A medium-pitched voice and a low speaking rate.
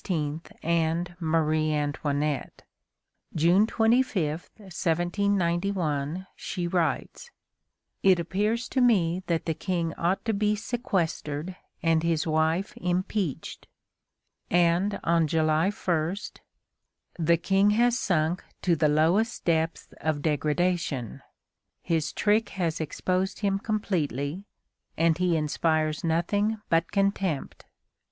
Yes: medium, 170 Hz; slow, 105 wpm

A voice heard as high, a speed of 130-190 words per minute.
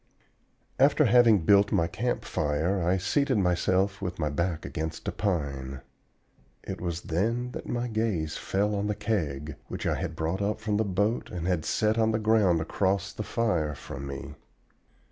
No: very low, 95 Hz; average, 180 wpm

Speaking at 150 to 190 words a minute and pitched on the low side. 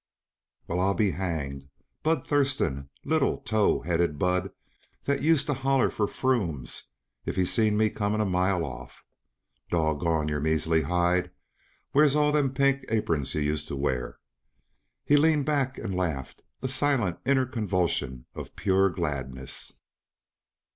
No: average, 140 wpm; very low, 95 Hz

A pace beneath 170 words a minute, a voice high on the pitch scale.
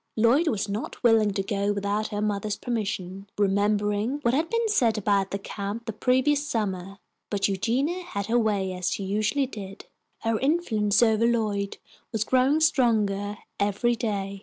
Yes: average, 160 wpm; high, 215 Hz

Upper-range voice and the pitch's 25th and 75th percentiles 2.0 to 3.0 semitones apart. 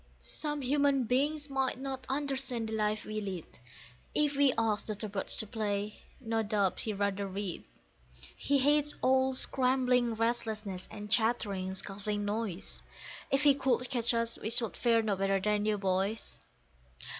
No: high, 225 Hz; average, 4.2 semitones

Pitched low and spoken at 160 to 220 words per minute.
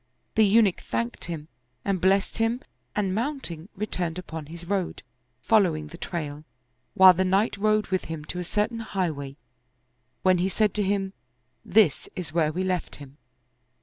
No: medium, 185 Hz; average, 175 wpm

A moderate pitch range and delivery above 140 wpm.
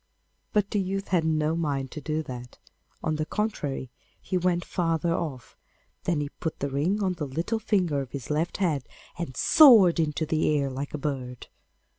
Yes: average, 4.2 semitones; average, 180 wpm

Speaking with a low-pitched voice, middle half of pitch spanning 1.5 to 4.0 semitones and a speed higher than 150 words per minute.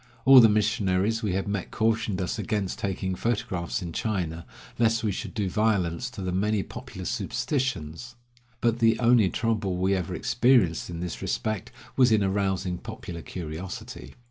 Yes: low, 100 Hz; average, 3.7 semitones; average, 160 wpm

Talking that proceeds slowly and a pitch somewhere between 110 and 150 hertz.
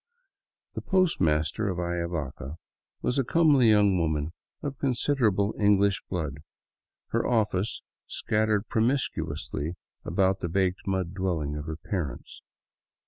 No: slow, 125 wpm; very low, 95 Hz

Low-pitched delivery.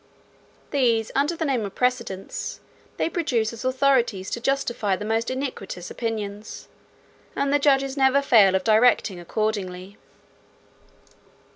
No: high, 230 Hz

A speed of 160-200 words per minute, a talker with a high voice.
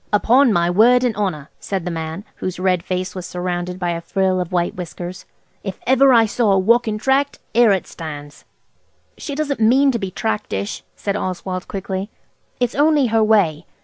Yes: average, 180 wpm; high, 195 Hz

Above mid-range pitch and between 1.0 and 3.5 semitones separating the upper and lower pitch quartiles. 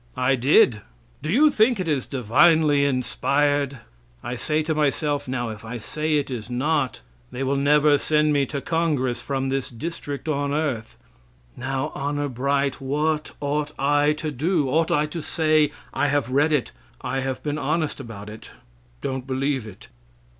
No: medium, 145 Hz; narrow, 2.6 semitones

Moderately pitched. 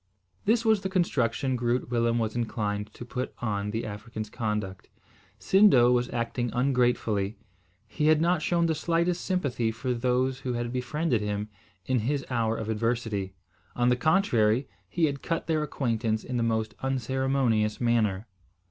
No: low, 120 Hz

